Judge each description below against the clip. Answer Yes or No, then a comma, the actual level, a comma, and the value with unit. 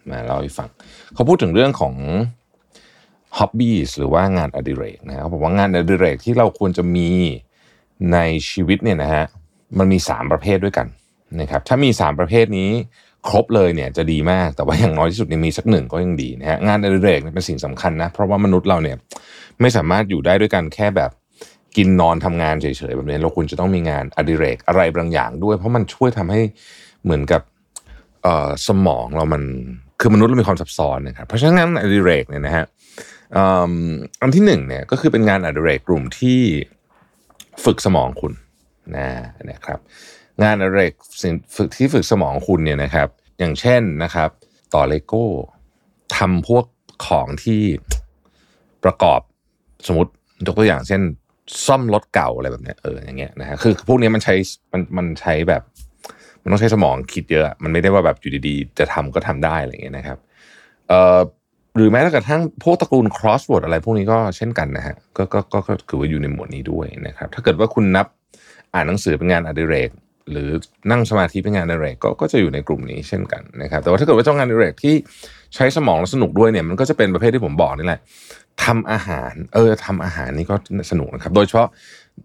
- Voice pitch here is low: Yes, very low, 95 Hz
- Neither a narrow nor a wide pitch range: No, wide, 5.7 semitones